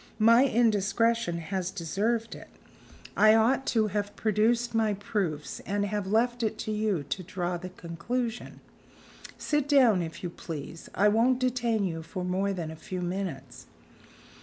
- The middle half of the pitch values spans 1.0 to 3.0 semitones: No, average, 4.3 semitones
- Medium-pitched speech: No, high, 205 Hz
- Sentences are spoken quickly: No, average, 155 wpm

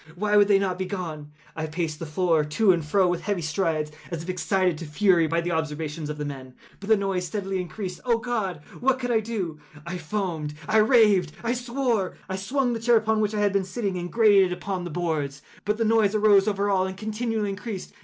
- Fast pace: Yes, fast, 220 wpm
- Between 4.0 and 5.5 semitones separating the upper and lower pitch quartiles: Yes, average, 4.4 semitones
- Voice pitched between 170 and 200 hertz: Yes, high, 190 Hz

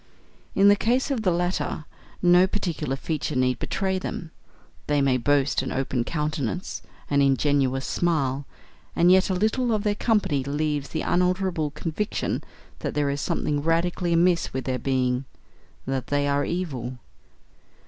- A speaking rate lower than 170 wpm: Yes, average, 155 wpm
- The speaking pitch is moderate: Yes, medium, 150 Hz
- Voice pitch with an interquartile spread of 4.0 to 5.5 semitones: Yes, average, 4.9 semitones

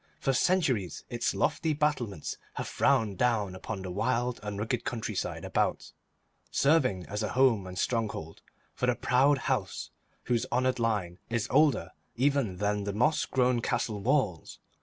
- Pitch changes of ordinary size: Yes, average, 4.2 semitones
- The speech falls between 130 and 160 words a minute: Yes, average, 150 wpm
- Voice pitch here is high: No, low, 115 Hz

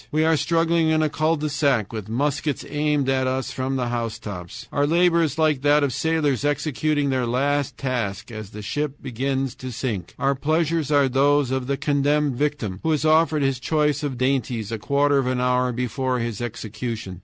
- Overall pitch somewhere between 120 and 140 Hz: Yes, low, 135 Hz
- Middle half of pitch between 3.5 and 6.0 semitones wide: No, average, 3.1 semitones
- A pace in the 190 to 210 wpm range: Yes, average, 195 wpm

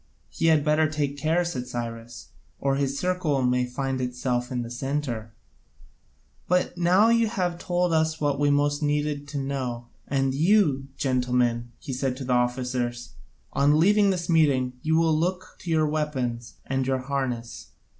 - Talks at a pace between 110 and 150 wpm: No, average, 165 wpm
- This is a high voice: No, medium, 140 Hz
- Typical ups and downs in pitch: Yes, average, 4.1 semitones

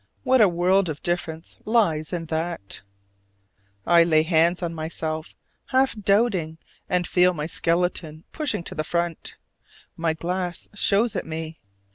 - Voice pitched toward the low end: No, medium, 170 Hz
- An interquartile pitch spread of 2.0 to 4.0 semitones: Yes, narrow, 2.6 semitones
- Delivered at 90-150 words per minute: Yes, average, 140 wpm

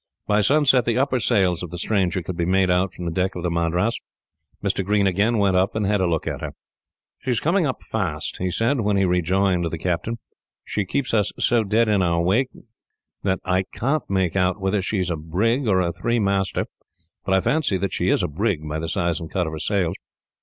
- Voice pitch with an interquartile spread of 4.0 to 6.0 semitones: No, average, 3.6 semitones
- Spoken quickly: Yes, fast, 230 wpm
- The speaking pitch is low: Yes, very low, 95 Hz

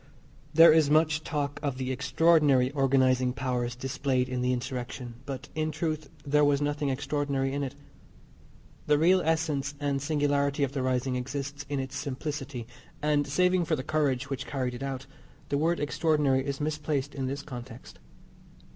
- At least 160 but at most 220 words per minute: Yes, average, 165 wpm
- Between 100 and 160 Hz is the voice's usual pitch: Yes, medium, 140 Hz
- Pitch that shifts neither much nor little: No, narrow, 2.3 semitones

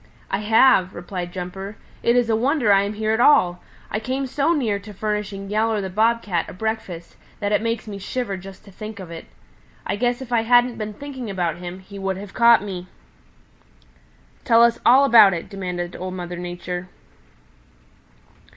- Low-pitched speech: No, high, 205 Hz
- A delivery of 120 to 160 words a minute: No, average, 185 wpm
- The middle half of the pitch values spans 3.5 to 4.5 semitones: Yes, average, 3.8 semitones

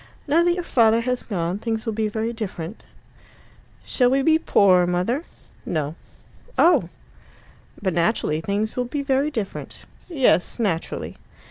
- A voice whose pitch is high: Yes, high, 225 Hz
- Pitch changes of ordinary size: No, wide, 6.4 semitones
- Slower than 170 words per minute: Yes, average, 140 wpm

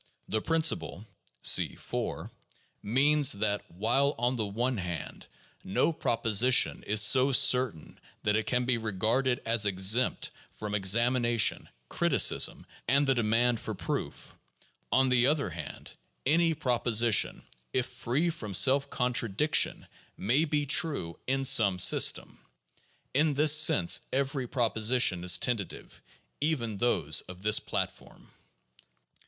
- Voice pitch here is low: Yes, low, 120 Hz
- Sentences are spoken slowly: Yes, slow, 125 wpm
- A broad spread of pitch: No, average, 4.3 semitones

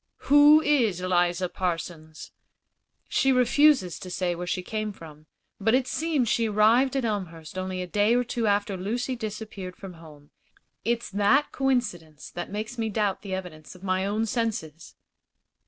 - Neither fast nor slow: Yes, average, 160 wpm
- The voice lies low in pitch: No, high, 205 Hz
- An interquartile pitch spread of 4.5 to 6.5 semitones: Yes, average, 4.8 semitones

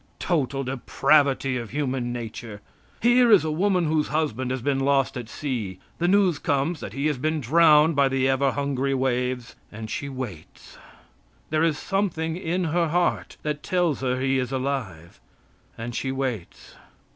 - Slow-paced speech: No, average, 165 wpm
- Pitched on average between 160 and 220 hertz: No, medium, 140 Hz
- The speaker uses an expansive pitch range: No, average, 3.9 semitones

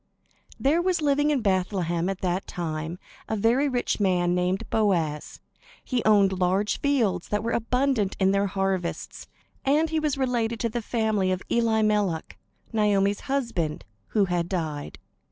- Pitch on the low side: No, high, 205 Hz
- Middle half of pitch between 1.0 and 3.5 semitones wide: No, average, 4.7 semitones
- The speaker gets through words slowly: No, average, 150 wpm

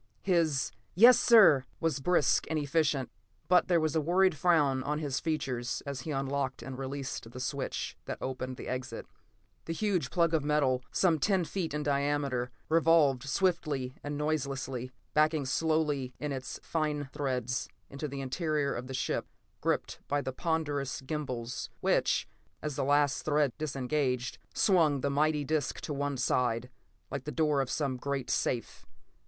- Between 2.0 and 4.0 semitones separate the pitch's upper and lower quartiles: Yes, average, 3.0 semitones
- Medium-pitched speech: Yes, medium, 145 Hz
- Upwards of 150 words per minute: Yes, average, 160 wpm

